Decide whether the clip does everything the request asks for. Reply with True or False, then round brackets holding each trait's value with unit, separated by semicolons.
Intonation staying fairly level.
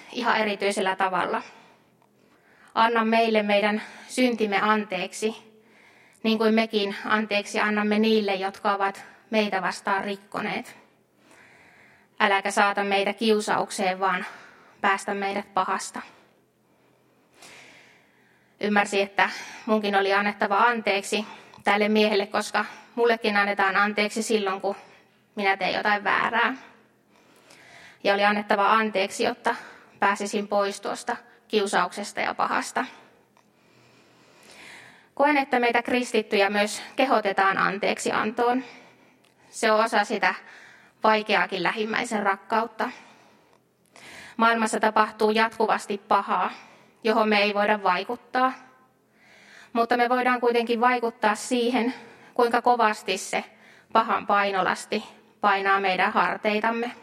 True (2.3 semitones)